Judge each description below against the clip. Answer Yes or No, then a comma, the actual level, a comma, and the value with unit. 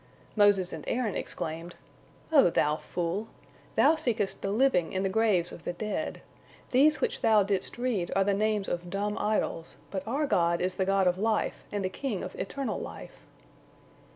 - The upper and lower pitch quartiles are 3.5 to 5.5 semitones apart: Yes, average, 3.8 semitones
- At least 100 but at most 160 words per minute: No, average, 180 wpm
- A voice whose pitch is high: Yes, high, 200 Hz